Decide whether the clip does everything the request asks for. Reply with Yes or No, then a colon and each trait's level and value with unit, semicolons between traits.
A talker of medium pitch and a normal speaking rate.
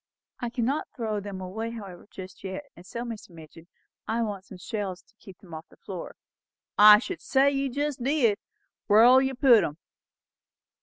No: high, 215 Hz; average, 175 wpm